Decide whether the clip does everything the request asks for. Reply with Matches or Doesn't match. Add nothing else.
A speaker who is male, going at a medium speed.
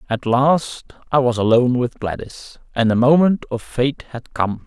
Matches